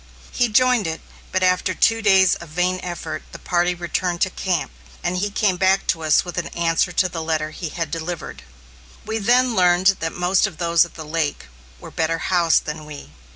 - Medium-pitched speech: Yes, medium, 175 Hz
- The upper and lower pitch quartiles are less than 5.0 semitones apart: Yes, narrow, 2.4 semitones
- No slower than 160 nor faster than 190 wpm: No, average, 200 wpm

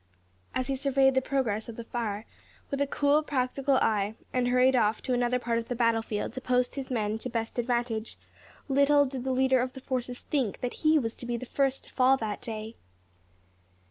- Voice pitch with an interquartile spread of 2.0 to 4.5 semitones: Yes, narrow, 2.5 semitones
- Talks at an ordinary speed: No, fast, 210 wpm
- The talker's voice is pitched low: No, very high, 250 Hz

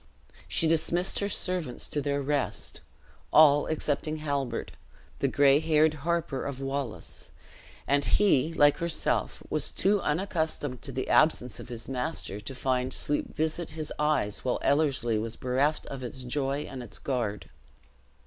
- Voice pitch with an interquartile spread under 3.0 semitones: No, average, 3.4 semitones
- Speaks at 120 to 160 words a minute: Yes, average, 150 wpm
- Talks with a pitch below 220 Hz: Yes, medium, 140 Hz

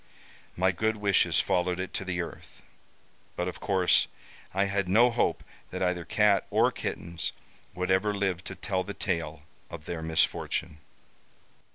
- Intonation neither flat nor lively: No, narrow, 2.3 semitones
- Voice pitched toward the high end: No, very low, 95 Hz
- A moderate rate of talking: Yes, average, 155 wpm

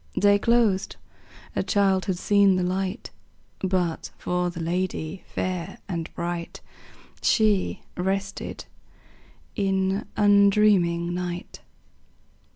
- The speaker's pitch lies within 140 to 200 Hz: Yes, high, 190 Hz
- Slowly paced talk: Yes, slow, 95 wpm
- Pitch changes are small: Yes, narrow, 2.2 semitones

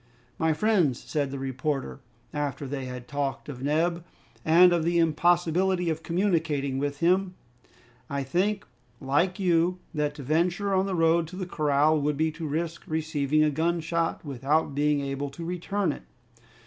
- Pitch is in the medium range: Yes, medium, 160 Hz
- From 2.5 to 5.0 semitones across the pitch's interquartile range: Yes, average, 3.3 semitones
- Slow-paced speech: No, average, 160 wpm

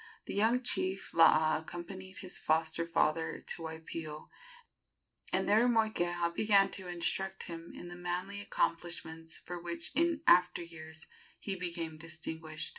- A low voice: No, medium, 175 Hz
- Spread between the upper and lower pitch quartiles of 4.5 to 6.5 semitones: No, average, 2.8 semitones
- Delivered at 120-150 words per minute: Yes, slow, 135 wpm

